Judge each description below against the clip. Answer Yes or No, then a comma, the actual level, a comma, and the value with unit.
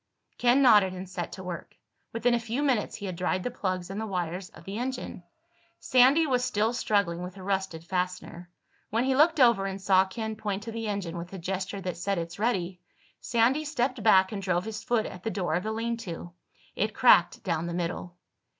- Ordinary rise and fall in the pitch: Yes, average, 4.3 semitones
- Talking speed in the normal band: No, fast, 215 wpm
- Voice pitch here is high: Yes, high, 195 Hz